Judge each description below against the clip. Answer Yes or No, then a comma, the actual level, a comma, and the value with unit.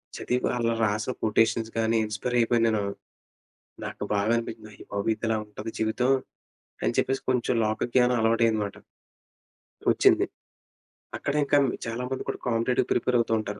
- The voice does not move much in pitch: Yes, narrow, 2.1 semitones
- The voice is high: No, low, 115 Hz